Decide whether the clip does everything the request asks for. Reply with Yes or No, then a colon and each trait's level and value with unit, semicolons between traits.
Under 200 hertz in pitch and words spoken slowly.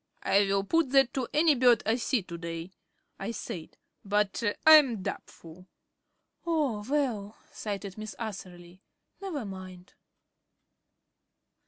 No: high, 210 Hz; slow, 125 wpm